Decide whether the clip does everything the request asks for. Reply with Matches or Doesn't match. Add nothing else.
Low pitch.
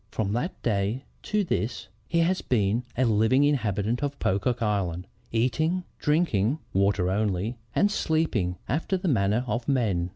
Matches